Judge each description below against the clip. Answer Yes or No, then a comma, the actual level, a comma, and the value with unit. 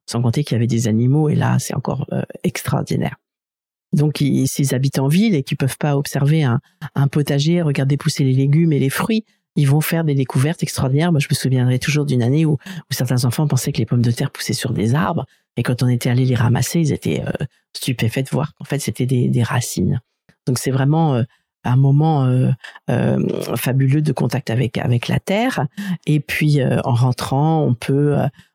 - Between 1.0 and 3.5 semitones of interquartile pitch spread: Yes, average, 3.2 semitones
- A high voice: No, medium, 140 Hz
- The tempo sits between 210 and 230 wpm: Yes, average, 215 wpm